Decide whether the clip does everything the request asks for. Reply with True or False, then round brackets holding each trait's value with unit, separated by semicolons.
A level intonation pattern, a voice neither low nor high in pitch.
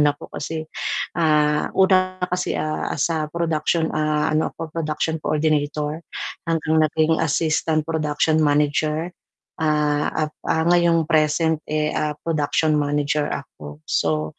True (1.3 semitones; 155 Hz)